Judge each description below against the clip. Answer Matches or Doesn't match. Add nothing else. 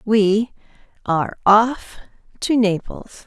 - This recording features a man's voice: Doesn't match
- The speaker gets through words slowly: Matches